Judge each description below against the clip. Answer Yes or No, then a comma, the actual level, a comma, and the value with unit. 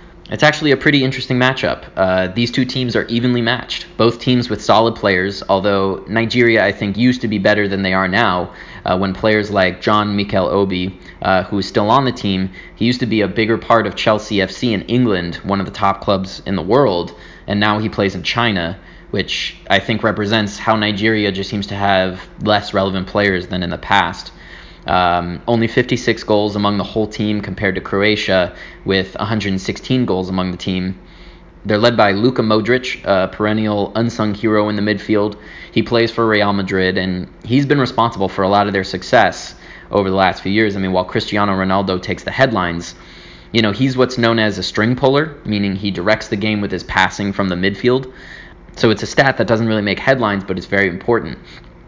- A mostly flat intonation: No, average, 3.1 semitones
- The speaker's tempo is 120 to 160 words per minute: No, fast, 205 wpm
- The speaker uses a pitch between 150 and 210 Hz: No, low, 105 Hz